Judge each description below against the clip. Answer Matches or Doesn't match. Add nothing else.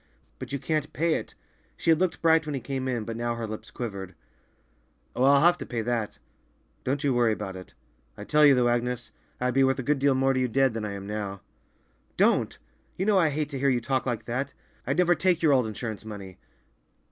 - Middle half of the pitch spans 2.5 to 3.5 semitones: Doesn't match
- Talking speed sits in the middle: Doesn't match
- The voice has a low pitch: Matches